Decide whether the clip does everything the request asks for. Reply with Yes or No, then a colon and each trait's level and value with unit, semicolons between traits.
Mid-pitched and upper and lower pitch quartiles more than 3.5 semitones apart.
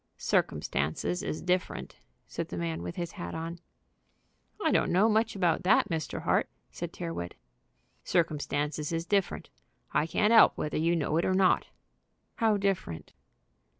Yes: medium, 170 Hz; average, 4.2 semitones